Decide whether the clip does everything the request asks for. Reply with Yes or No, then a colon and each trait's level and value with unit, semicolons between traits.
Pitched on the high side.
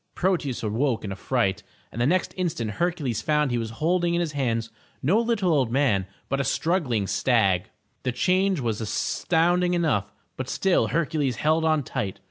No: medium, 140 Hz